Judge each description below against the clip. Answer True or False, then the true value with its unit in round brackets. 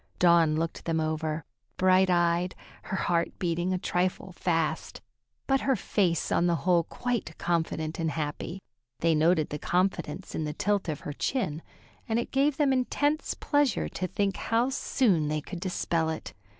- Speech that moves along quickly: False (165 wpm)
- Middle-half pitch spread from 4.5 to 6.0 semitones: False (3.6 semitones)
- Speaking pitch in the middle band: True (175 Hz)